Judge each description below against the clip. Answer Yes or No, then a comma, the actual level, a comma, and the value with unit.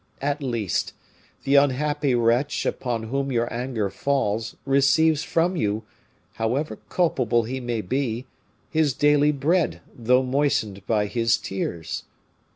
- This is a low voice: Yes, low, 130 Hz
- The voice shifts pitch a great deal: No, average, 3.9 semitones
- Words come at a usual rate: No, slow, 125 wpm